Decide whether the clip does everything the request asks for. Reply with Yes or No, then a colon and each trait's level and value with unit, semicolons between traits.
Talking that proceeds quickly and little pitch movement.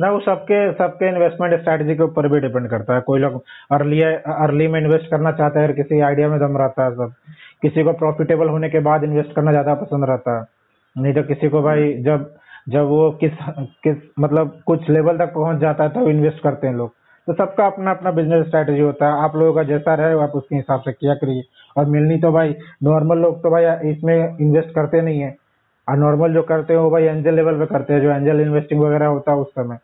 Yes: fast, 230 wpm; narrow, 2.0 semitones